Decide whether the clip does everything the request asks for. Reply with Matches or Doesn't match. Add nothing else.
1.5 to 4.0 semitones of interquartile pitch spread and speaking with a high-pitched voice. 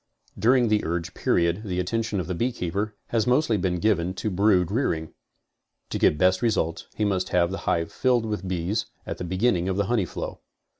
Doesn't match